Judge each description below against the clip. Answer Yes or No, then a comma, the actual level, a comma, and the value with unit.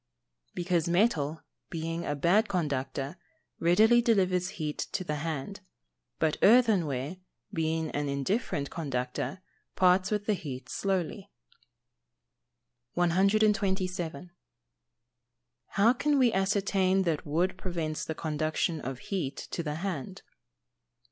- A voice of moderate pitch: Yes, medium, 175 Hz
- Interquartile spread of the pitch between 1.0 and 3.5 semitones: No, average, 4.2 semitones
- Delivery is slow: Yes, slow, 110 wpm